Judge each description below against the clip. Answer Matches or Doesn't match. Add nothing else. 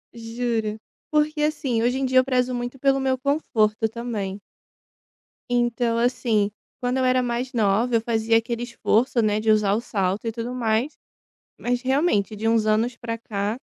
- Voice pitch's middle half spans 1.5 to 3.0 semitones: Matches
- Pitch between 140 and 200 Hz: Doesn't match